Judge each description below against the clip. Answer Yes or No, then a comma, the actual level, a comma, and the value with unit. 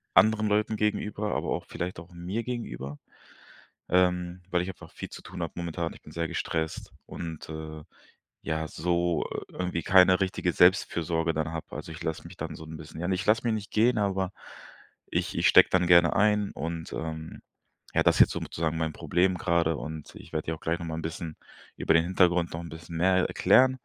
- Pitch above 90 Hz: No, very low, 85 Hz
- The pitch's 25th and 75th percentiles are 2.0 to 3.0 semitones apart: Yes, narrow, 2.5 semitones